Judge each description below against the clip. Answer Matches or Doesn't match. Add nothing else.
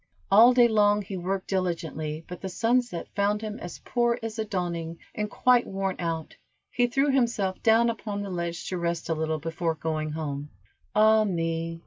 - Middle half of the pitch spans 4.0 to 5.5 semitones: Matches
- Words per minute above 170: Matches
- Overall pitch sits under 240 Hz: Matches